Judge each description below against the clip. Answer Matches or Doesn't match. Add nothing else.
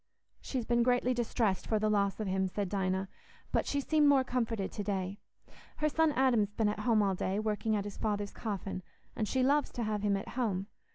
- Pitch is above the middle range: Matches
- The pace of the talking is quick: Matches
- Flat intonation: Doesn't match